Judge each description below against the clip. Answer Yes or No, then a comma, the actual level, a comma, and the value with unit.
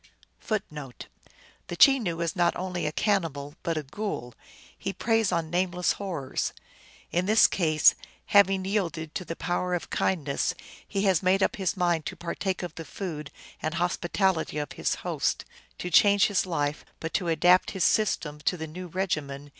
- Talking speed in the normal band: Yes, average, 170 wpm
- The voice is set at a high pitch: No, medium, 175 Hz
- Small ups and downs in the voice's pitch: No, average, 3.4 semitones